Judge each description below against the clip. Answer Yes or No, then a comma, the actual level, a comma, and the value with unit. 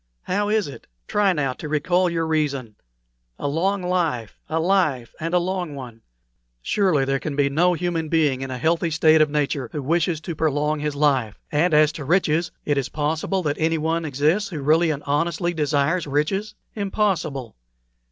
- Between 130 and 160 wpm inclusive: No, average, 180 wpm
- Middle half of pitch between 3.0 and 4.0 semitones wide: Yes, average, 3.3 semitones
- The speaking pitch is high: No, medium, 155 Hz